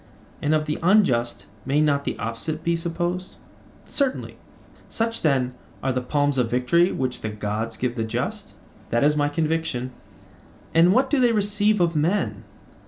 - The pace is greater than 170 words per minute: No, average, 165 wpm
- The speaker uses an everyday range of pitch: No, wide, 6.1 semitones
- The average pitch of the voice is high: No, medium, 150 Hz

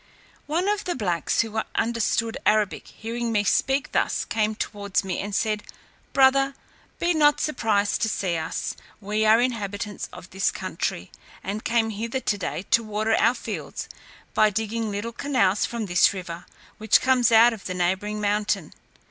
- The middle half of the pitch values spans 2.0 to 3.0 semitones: Yes, narrow, 2.5 semitones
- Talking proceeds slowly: No, average, 165 wpm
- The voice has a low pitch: No, high, 215 Hz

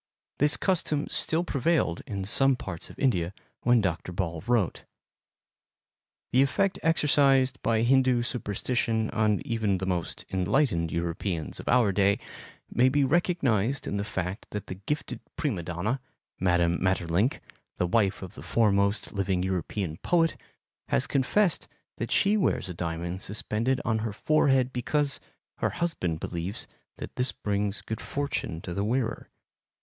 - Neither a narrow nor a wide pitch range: No, wide, 6.3 semitones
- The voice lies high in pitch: No, low, 110 Hz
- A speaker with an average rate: Yes, average, 145 wpm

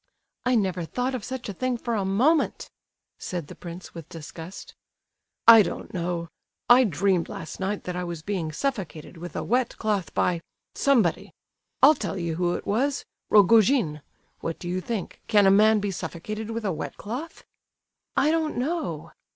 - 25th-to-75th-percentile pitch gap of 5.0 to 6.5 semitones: Yes, wide, 5.5 semitones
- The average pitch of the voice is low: No, high, 200 Hz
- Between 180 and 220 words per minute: No, average, 165 wpm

